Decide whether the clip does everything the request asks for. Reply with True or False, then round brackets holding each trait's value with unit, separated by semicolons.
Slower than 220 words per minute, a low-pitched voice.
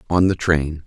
True (210 wpm; 80 Hz)